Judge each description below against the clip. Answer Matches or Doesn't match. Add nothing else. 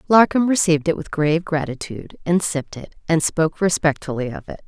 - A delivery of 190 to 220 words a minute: Doesn't match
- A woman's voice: Matches